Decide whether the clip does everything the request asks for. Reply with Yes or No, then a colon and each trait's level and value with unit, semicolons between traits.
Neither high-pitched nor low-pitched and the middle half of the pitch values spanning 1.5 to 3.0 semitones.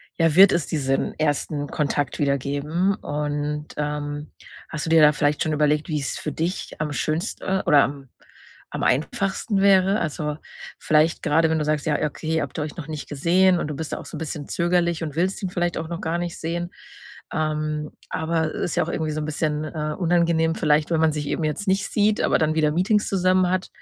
Yes: medium, 155 Hz; narrow, 2.5 semitones